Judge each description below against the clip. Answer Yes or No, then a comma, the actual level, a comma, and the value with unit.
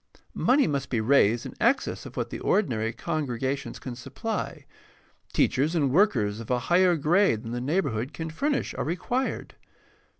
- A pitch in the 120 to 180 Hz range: Yes, medium, 140 Hz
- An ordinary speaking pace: Yes, average, 160 wpm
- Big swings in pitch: Yes, wide, 6.8 semitones